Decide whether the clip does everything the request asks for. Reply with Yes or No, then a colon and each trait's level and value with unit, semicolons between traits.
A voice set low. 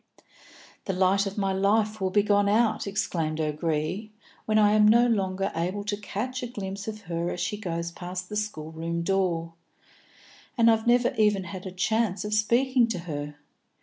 No: high, 200 Hz